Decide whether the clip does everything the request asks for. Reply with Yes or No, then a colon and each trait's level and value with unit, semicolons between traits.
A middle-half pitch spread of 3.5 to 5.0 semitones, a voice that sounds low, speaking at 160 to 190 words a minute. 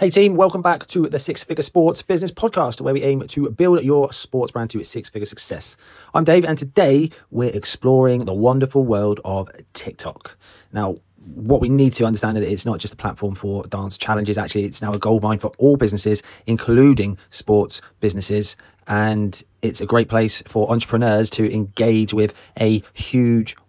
Yes: average, 4.6 semitones; low, 110 Hz; average, 185 wpm